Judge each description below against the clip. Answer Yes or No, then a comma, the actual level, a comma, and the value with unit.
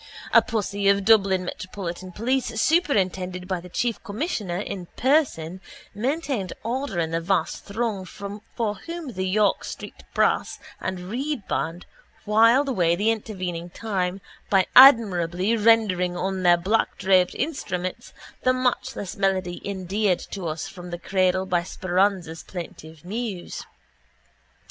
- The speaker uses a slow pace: Yes, slow, 130 wpm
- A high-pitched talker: Yes, high, 195 Hz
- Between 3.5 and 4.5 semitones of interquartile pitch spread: Yes, average, 3.9 semitones